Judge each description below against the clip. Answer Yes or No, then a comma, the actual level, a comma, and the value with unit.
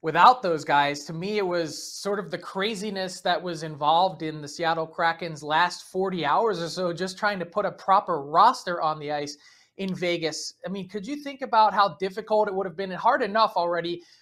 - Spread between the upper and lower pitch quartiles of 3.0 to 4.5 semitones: Yes, average, 3.5 semitones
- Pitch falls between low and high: Yes, medium, 180 Hz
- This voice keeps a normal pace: No, fast, 215 wpm